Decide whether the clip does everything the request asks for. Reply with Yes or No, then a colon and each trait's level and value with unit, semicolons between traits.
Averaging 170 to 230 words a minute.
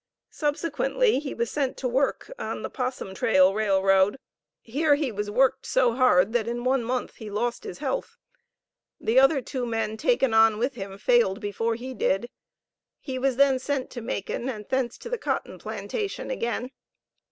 Yes: average, 175 wpm